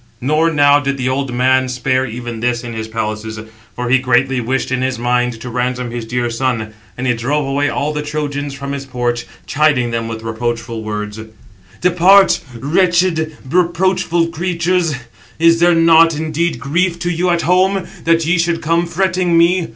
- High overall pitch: No, medium, 140 Hz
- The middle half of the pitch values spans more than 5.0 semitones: Yes, wide, 5.4 semitones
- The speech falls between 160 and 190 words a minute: Yes, average, 175 wpm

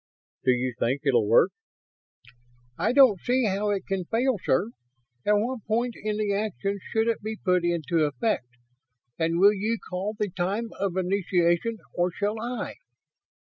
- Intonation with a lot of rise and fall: No, average, 4.2 semitones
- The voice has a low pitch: No, high, 200 Hz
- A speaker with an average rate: Yes, average, 160 wpm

